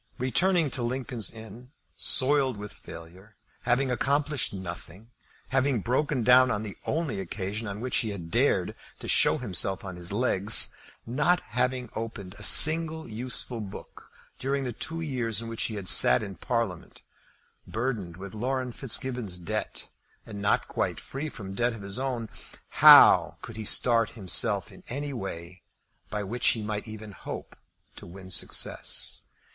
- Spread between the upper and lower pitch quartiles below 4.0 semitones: No, average, 4.6 semitones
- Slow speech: No, average, 155 wpm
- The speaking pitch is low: Yes, low, 115 Hz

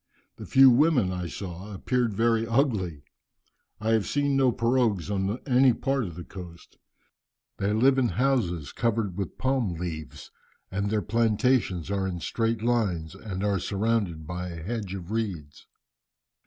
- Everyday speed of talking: Yes, average, 155 wpm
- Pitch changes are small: No, average, 5.0 semitones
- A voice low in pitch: Yes, low, 105 Hz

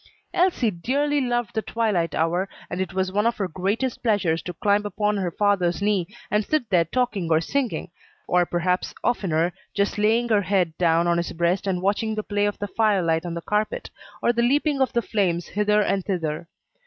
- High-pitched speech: Yes, high, 200 Hz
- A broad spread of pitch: No, average, 4.0 semitones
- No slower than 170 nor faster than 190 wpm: No, fast, 205 wpm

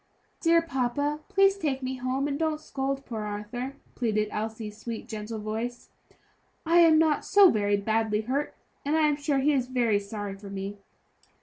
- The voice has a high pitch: Yes, very high, 250 Hz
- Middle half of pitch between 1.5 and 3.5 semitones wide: No, wide, 5.5 semitones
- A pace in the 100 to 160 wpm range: No, average, 175 wpm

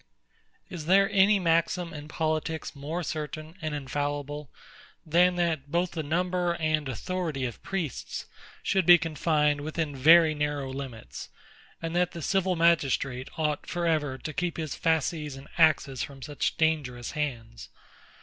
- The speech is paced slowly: No, average, 145 wpm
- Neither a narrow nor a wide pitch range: Yes, average, 3.0 semitones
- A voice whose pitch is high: No, medium, 155 Hz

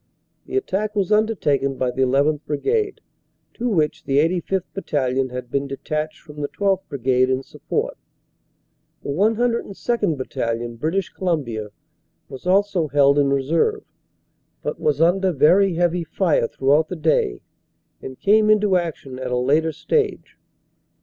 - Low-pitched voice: No, medium, 155 Hz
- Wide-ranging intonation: Yes, wide, 6.1 semitones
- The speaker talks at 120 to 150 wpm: Yes, average, 145 wpm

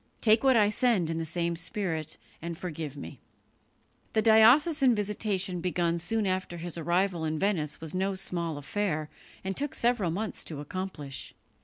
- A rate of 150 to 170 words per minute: Yes, average, 160 wpm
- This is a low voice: No, medium, 185 Hz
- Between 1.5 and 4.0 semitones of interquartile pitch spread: No, average, 4.4 semitones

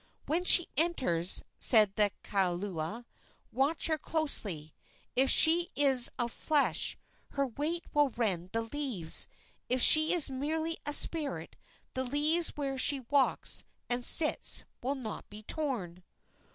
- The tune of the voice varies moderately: No, wide, 6.1 semitones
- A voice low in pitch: No, very high, 270 Hz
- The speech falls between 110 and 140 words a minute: Yes, slow, 135 wpm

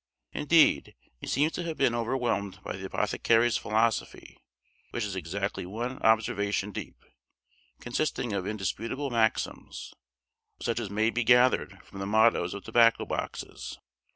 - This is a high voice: No, low, 115 Hz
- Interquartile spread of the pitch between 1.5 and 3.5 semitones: Yes, average, 3.1 semitones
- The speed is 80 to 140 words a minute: Yes, slow, 135 wpm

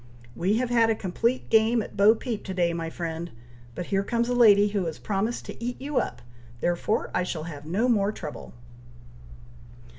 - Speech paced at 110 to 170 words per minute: No, average, 190 wpm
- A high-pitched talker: Yes, high, 200 Hz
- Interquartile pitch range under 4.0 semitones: No, average, 5.1 semitones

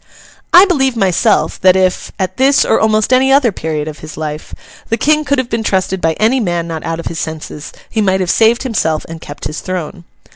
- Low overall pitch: No, high, 190 Hz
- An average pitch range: No, wide, 6.5 semitones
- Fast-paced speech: Yes, fast, 220 wpm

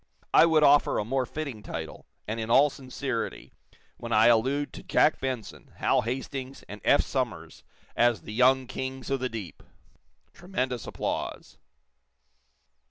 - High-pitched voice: No, low, 130 Hz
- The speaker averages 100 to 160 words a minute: Yes, average, 145 wpm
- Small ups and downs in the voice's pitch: No, average, 3.2 semitones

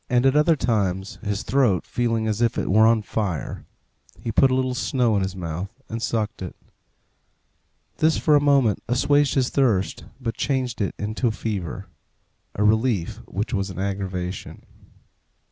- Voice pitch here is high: No, low, 110 Hz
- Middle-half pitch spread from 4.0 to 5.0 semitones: Yes, average, 4.6 semitones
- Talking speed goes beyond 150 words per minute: Yes, average, 160 wpm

